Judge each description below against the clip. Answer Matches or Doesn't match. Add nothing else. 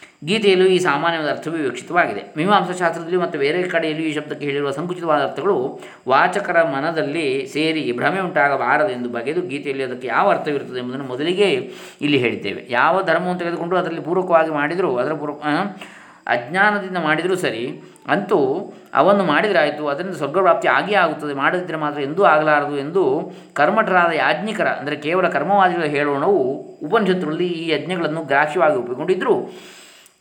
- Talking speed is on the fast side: Matches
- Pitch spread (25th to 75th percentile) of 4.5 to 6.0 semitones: Doesn't match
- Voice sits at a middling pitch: Matches